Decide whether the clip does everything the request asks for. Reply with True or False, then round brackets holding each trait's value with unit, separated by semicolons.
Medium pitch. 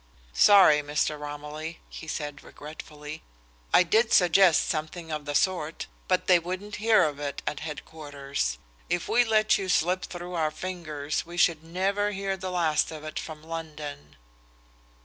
True (160 Hz)